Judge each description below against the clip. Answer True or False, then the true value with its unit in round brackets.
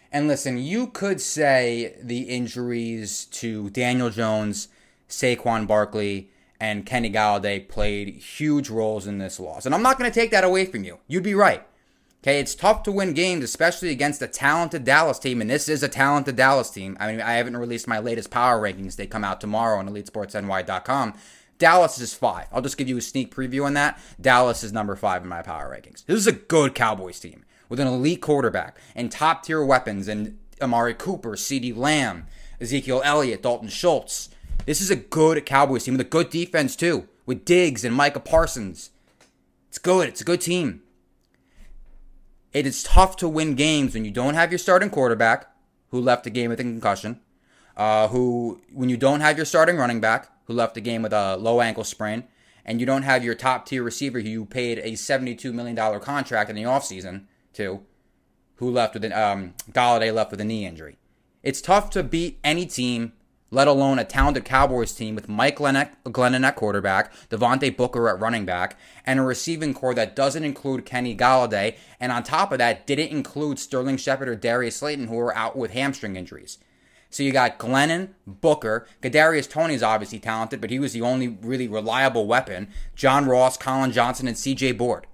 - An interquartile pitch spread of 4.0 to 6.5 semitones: True (4.5 semitones)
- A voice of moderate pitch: False (125 Hz)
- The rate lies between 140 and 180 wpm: False (195 wpm)